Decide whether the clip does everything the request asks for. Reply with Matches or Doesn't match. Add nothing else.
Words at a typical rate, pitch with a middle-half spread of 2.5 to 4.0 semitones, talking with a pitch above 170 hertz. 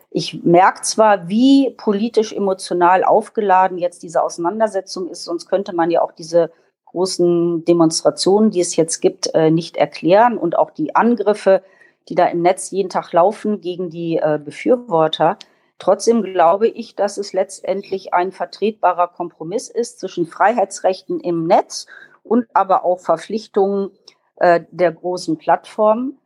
Matches